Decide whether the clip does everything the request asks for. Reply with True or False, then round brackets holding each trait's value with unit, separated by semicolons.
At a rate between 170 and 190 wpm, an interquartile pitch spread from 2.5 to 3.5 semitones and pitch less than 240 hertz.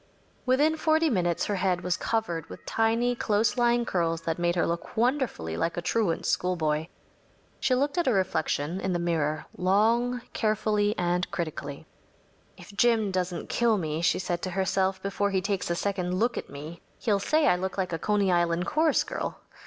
False (185 wpm; 4.8 semitones; 190 Hz)